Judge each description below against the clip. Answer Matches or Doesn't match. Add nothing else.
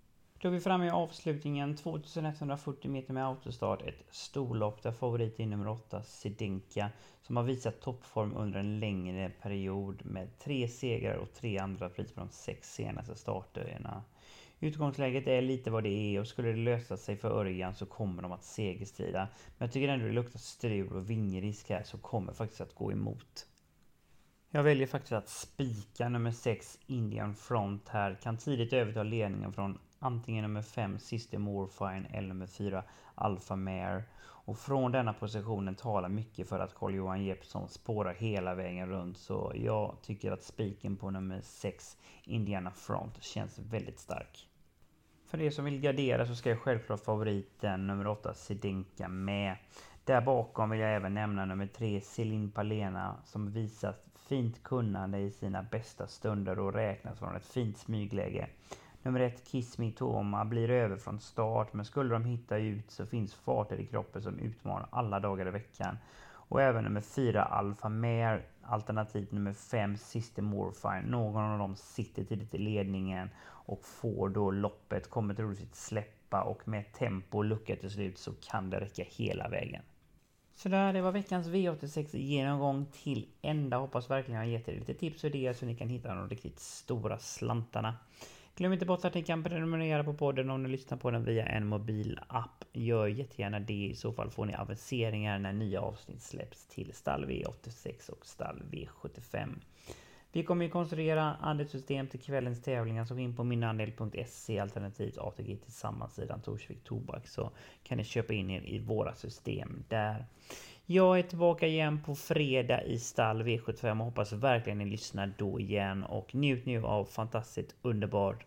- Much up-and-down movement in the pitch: Doesn't match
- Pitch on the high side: Doesn't match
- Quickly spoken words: Doesn't match